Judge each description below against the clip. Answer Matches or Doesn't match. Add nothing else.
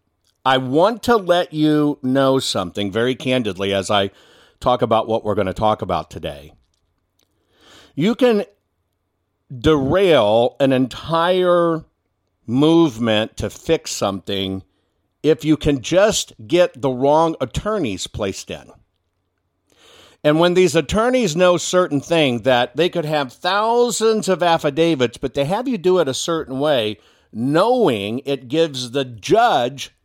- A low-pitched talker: Matches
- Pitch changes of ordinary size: Doesn't match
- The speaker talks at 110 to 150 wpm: Matches